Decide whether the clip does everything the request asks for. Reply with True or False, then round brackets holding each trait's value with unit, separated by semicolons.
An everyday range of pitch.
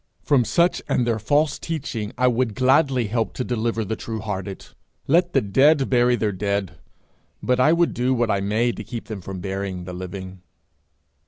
True (4.4 semitones)